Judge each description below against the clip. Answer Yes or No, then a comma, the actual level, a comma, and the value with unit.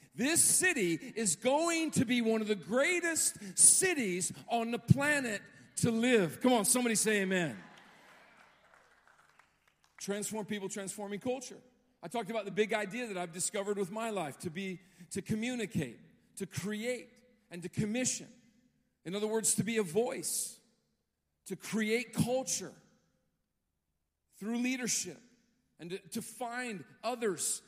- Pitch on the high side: Yes, high, 220 Hz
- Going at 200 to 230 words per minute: No, slow, 135 wpm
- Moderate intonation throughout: Yes, average, 4.1 semitones